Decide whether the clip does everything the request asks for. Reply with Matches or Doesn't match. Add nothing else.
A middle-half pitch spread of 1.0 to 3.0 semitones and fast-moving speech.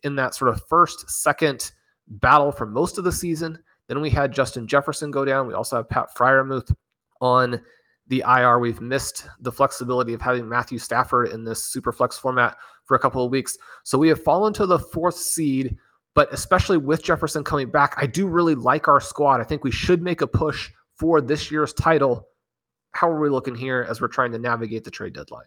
Doesn't match